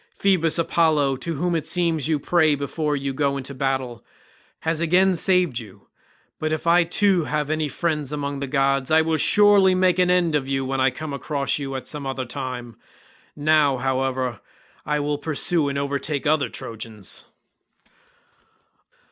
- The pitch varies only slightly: No, average, 3.3 semitones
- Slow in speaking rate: No, average, 165 wpm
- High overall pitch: No, medium, 145 Hz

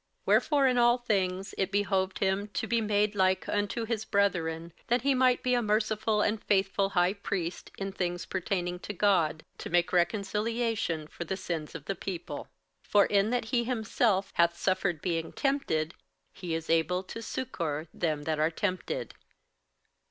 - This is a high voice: Yes, high, 195 Hz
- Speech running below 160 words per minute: No, average, 175 wpm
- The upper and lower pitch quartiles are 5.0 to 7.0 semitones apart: No, average, 3.9 semitones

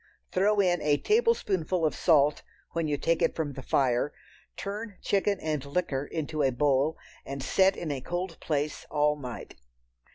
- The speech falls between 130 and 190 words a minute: Yes, average, 165 wpm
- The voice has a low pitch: No, medium, 155 Hz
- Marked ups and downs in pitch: No, average, 4.5 semitones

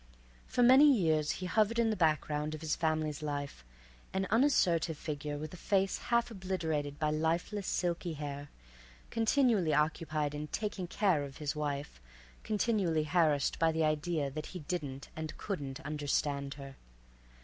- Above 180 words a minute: No, average, 150 wpm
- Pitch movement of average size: Yes, average, 4.2 semitones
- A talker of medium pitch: Yes, medium, 155 Hz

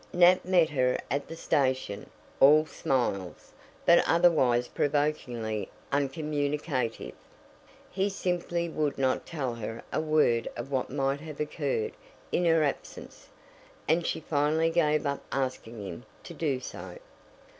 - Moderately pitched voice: Yes, medium, 145 Hz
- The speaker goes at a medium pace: No, slow, 130 wpm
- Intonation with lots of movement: No, average, 4.1 semitones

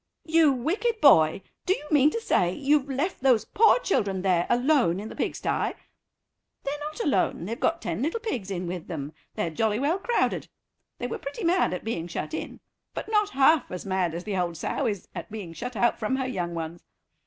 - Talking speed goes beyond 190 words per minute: Yes, fast, 205 wpm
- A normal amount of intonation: No, wide, 9.0 semitones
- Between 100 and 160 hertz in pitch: No, high, 240 Hz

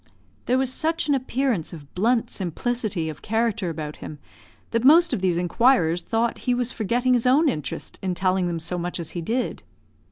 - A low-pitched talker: No, high, 225 Hz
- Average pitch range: No, wide, 6.4 semitones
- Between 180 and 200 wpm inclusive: Yes, average, 190 wpm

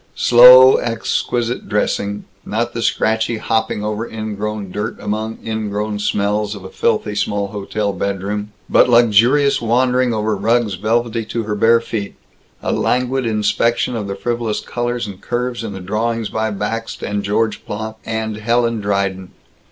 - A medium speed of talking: Yes, average, 150 wpm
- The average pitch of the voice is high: No, low, 110 Hz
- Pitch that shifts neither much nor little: No, narrow, 2.2 semitones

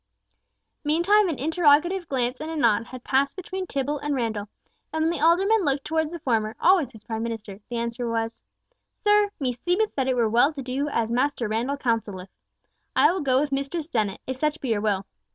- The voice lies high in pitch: Yes, very high, 275 Hz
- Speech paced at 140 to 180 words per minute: No, average, 200 wpm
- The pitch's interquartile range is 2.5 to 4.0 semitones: No, wide, 5.5 semitones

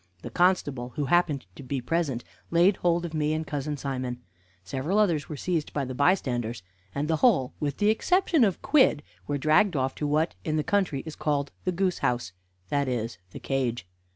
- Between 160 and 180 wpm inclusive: No, average, 195 wpm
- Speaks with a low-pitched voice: No, medium, 150 Hz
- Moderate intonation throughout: Yes, average, 4.7 semitones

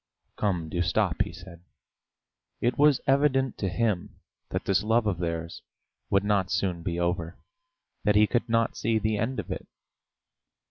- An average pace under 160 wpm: No, average, 165 wpm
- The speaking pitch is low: Yes, low, 100 Hz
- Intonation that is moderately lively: Yes, average, 4.8 semitones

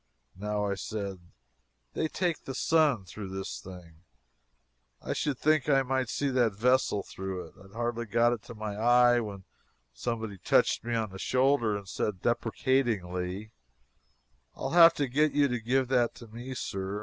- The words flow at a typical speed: Yes, average, 175 wpm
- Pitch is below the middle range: Yes, low, 115 Hz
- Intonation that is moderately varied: Yes, average, 4.6 semitones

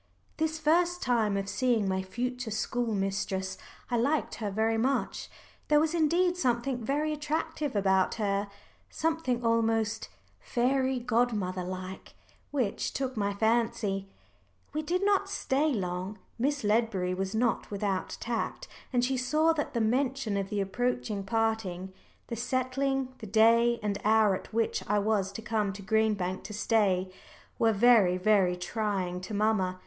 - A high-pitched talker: Yes, high, 225 Hz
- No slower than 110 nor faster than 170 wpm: Yes, average, 150 wpm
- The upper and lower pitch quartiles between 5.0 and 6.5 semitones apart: No, average, 4.5 semitones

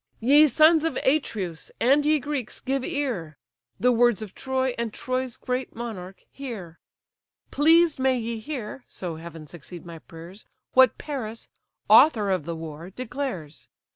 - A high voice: Yes, high, 235 Hz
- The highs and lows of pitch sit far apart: Yes, wide, 7.0 semitones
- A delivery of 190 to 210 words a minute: No, average, 145 wpm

